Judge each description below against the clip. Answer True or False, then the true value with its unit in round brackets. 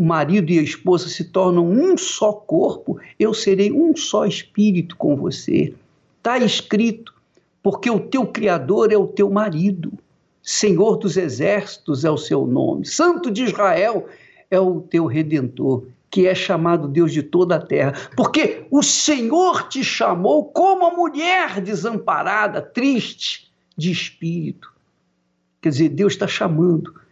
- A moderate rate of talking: True (145 wpm)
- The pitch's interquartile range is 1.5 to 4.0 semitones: False (5.1 semitones)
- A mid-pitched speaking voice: False (195 Hz)